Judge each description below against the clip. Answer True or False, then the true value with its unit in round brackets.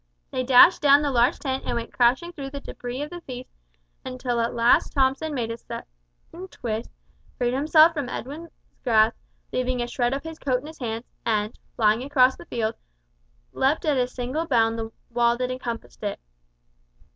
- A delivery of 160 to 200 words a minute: True (180 wpm)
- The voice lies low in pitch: False (255 Hz)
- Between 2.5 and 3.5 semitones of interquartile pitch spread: True (3.1 semitones)